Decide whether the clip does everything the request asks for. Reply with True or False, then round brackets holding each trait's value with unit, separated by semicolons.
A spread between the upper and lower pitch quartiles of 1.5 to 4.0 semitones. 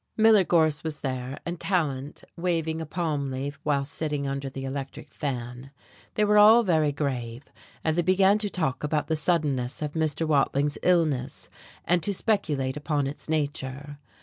True (3.5 semitones)